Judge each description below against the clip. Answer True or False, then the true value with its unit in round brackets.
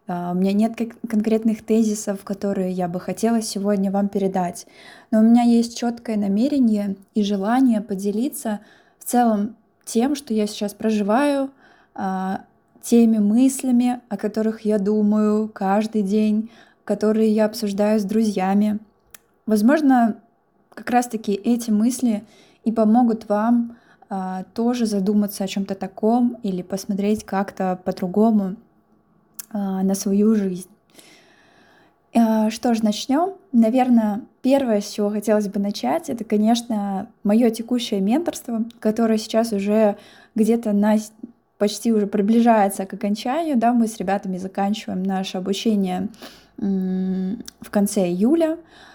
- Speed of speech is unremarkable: True (125 wpm)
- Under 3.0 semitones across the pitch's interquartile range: True (2.6 semitones)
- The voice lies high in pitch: True (215 Hz)